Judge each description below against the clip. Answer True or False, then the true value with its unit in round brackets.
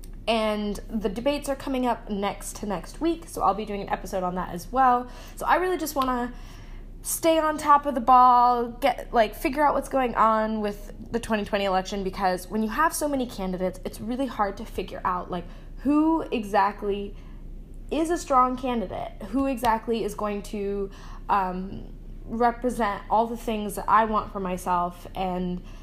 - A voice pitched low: False (220 Hz)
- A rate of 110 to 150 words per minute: False (185 wpm)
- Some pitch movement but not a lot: True (4.2 semitones)